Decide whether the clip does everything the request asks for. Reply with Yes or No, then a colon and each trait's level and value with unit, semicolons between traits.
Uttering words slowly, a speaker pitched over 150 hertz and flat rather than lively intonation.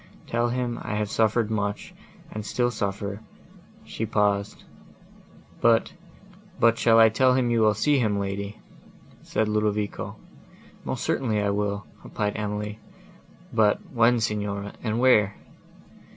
No: slow, 125 wpm; low, 105 Hz; narrow, 2.1 semitones